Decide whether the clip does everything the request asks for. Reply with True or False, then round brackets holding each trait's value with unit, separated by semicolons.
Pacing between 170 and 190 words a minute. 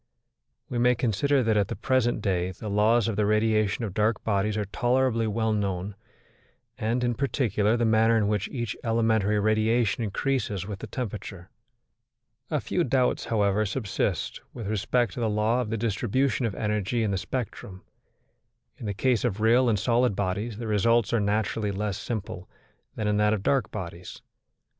True (175 wpm)